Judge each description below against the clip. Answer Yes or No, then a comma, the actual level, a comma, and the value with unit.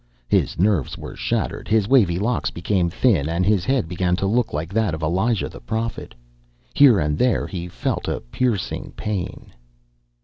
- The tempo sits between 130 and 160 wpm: No, average, 170 wpm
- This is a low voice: Yes, very low, 95 Hz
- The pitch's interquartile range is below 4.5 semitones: No, average, 4.8 semitones